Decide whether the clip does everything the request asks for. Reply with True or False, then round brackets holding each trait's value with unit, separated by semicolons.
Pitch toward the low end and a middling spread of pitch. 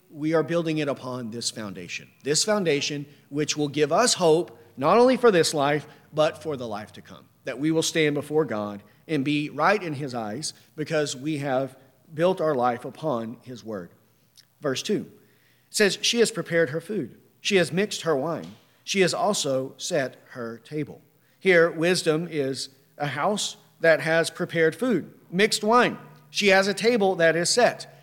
False (155 Hz; 4.3 semitones)